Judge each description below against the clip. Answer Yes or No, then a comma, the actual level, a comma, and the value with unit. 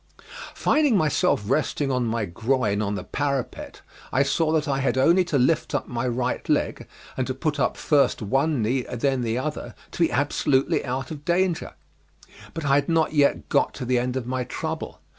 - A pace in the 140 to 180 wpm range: No, average, 200 wpm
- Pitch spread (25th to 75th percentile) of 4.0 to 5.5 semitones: No, average, 3.6 semitones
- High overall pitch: No, low, 135 Hz